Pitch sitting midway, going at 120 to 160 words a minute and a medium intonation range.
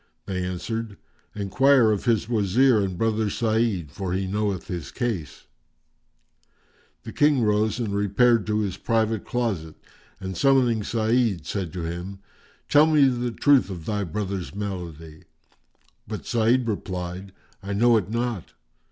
No: low, 105 Hz; average, 140 wpm; average, 3.8 semitones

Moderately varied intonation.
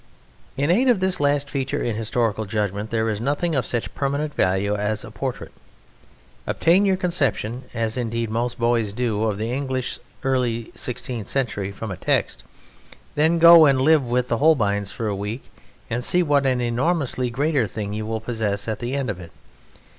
Yes: average, 4.6 semitones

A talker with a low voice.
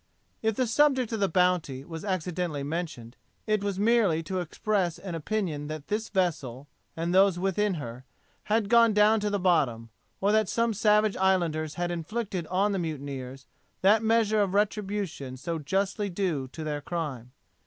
No: medium, 185 Hz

